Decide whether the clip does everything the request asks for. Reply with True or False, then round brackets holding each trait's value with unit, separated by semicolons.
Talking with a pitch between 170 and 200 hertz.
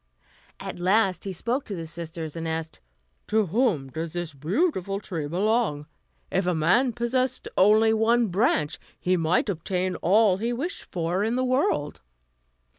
True (190 Hz)